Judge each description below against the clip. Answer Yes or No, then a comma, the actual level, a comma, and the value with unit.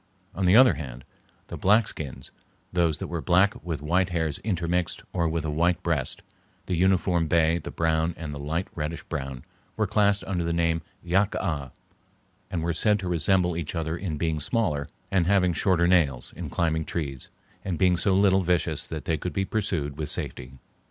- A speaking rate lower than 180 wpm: No, average, 190 wpm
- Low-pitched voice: Yes, very low, 85 Hz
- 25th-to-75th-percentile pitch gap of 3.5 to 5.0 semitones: No, average, 2.9 semitones